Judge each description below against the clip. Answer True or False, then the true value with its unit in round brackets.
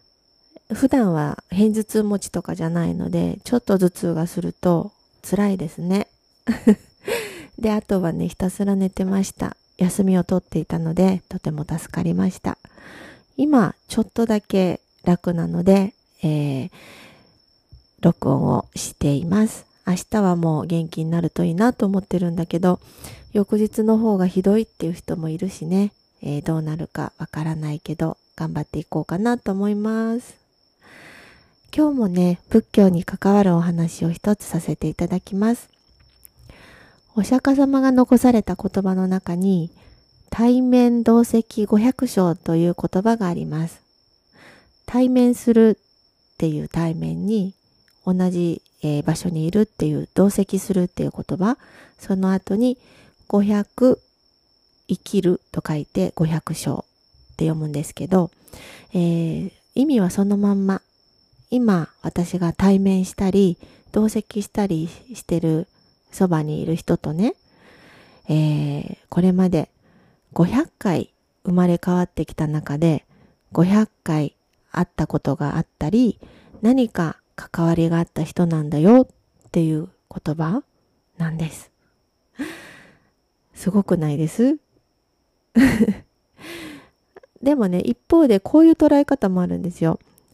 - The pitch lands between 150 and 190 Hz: True (185 Hz)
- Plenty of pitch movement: False (4.6 semitones)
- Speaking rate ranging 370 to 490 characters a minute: False (250 characters per minute)